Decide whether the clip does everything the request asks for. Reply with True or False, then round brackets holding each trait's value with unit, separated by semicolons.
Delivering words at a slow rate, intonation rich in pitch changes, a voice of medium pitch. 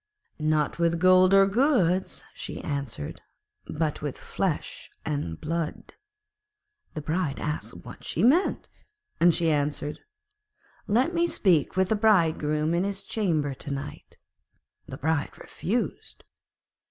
False (125 wpm; 4.5 semitones; 165 Hz)